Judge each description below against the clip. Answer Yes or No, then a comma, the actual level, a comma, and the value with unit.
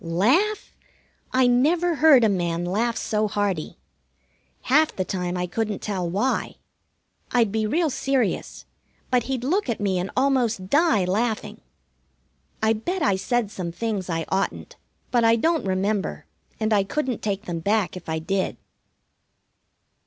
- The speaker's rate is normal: Yes, average, 150 wpm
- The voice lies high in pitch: Yes, high, 215 Hz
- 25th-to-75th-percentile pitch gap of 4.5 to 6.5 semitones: Yes, average, 5.2 semitones